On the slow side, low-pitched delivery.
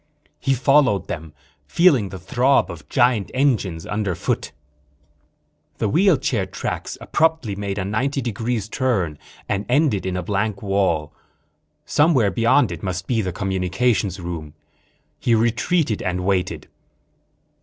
Yes: slow, 125 wpm; low, 105 Hz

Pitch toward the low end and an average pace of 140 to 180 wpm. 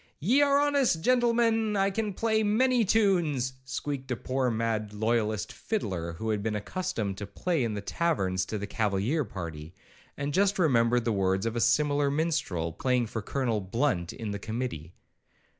Yes: low, 125 Hz; average, 170 wpm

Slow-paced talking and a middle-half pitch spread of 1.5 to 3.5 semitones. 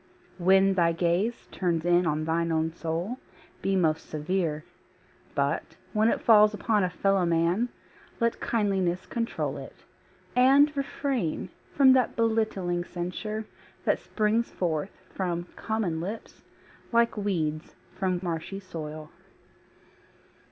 No: slow, 120 wpm; average, 4.7 semitones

